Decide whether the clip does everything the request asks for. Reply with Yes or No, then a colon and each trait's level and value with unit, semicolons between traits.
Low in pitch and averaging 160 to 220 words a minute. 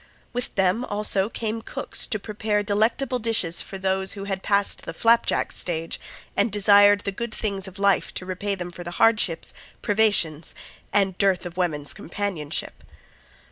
No: high, 200 Hz; average, 165 wpm